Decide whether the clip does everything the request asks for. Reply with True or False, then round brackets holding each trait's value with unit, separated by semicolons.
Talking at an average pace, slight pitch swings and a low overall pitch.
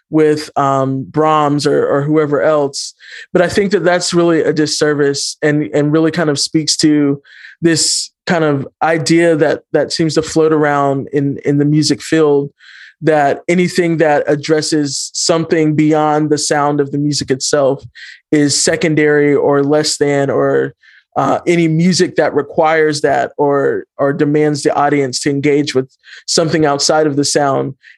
False (160 wpm; 2.0 semitones; 150 Hz)